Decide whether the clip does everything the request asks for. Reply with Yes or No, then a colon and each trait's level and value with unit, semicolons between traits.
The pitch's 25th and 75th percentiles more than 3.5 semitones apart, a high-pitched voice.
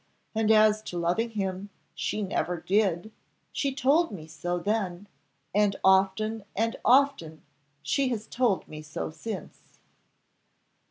Yes: average, 4.1 semitones; high, 205 Hz